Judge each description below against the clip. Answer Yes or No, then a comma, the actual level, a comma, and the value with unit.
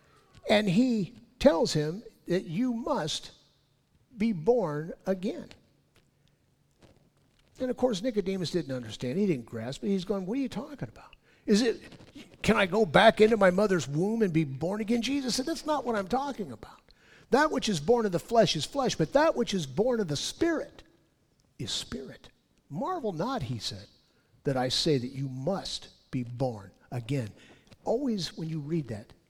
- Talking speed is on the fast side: No, average, 175 wpm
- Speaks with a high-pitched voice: Yes, high, 200 Hz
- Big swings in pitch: Yes, wide, 8.2 semitones